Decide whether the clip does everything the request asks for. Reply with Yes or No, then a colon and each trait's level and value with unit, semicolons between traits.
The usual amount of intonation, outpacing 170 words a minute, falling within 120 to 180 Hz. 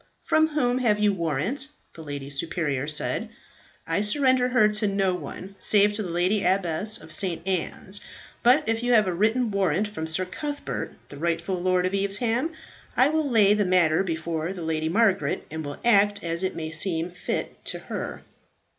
No: average, 4.6 semitones; average, 180 wpm; high, 195 Hz